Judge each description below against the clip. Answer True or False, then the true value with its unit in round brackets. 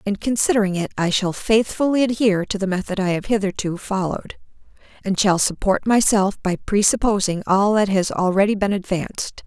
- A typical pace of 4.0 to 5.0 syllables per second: False (5.5 syllables/s)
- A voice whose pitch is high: True (200 Hz)